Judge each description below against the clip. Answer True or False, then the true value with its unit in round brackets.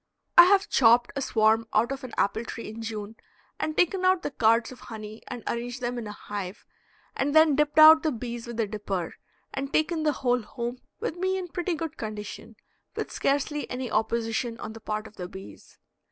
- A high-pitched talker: True (240 Hz)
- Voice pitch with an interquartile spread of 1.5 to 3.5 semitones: False (5.4 semitones)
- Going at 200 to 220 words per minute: True (205 wpm)